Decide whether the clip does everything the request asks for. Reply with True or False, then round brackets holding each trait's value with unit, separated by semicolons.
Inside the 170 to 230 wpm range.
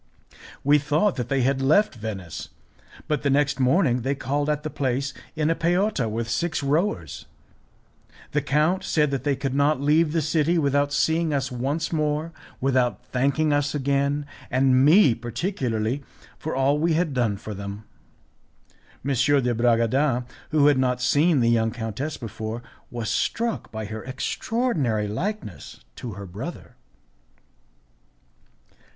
False (145 wpm)